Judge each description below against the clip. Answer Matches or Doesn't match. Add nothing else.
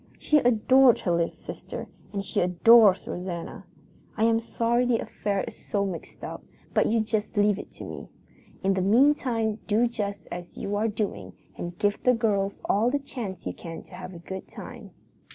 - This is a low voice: Doesn't match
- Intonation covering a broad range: Doesn't match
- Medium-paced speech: Matches